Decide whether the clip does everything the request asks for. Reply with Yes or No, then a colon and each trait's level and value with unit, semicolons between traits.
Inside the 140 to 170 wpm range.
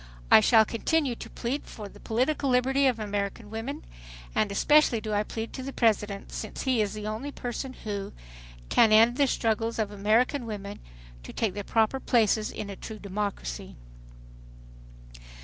Yes: average, 165 wpm